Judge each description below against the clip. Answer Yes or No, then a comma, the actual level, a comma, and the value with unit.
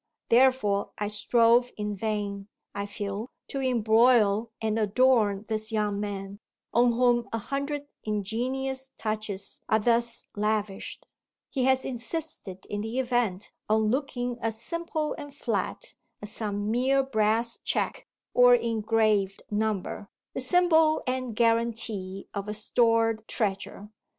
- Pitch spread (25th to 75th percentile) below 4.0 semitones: Yes, average, 3.2 semitones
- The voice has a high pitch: Yes, high, 225 Hz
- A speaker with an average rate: No, slow, 125 wpm